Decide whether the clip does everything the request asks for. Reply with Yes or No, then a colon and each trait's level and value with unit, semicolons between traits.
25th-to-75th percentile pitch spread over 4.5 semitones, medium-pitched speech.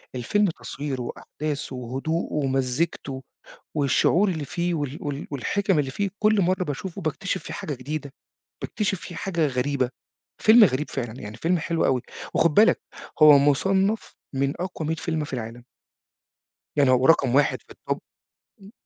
Yes: average, 4.9 semitones; medium, 150 Hz